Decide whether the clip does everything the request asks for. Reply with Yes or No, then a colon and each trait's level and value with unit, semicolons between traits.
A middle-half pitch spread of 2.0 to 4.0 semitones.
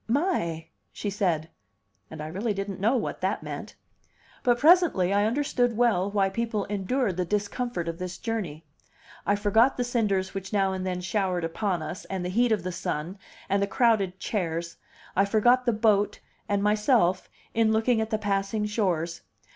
Yes: average, 3.6 semitones